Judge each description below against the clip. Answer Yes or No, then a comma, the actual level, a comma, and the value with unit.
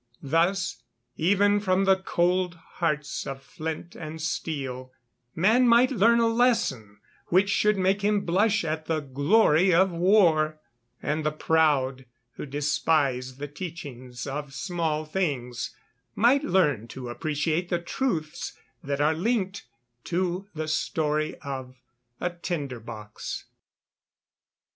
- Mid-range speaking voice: Yes, medium, 160 Hz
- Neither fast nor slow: No, slow, 125 wpm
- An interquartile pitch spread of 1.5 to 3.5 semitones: No, average, 4.9 semitones